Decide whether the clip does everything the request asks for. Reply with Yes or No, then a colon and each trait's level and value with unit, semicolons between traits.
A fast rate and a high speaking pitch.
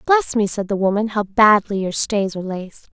Yes: fast, 225 wpm; high, 200 Hz